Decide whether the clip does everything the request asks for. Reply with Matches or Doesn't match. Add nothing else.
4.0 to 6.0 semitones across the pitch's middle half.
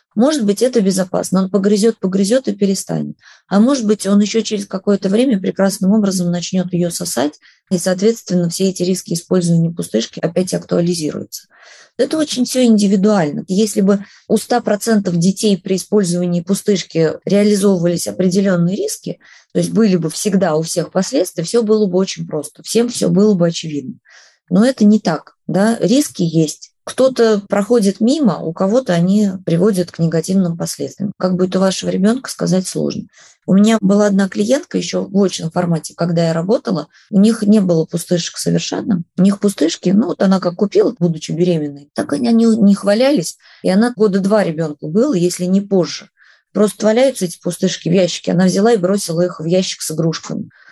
Doesn't match